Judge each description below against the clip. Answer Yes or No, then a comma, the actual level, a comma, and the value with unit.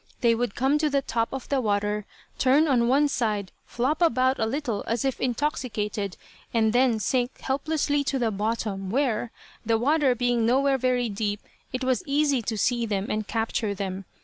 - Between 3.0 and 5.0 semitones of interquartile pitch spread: Yes, average, 3.8 semitones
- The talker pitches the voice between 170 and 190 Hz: No, high, 240 Hz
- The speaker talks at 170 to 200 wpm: Yes, average, 180 wpm